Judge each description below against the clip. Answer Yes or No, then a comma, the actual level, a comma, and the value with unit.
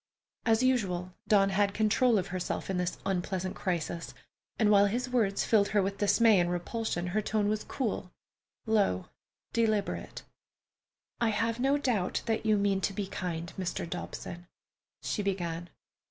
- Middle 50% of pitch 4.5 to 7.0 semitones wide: No, average, 3.5 semitones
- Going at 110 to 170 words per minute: Yes, average, 150 wpm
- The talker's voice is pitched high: Yes, high, 200 Hz